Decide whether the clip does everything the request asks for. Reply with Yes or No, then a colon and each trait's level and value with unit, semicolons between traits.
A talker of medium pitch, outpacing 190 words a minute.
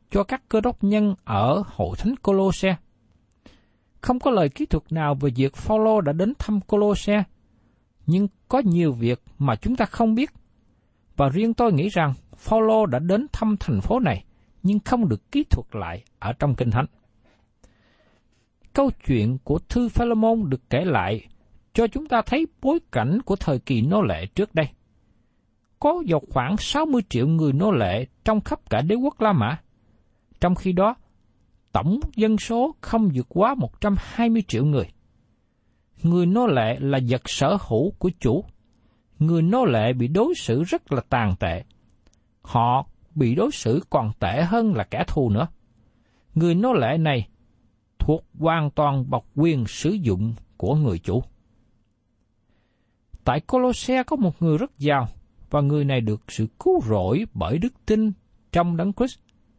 No: medium, 150 Hz; slow, 165 wpm